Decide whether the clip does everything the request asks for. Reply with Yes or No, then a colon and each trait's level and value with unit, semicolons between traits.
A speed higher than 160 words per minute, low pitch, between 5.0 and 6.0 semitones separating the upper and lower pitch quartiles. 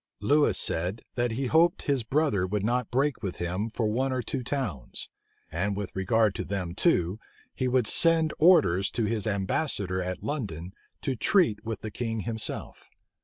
Yes: average, 170 wpm; low, 115 Hz; wide, 5.5 semitones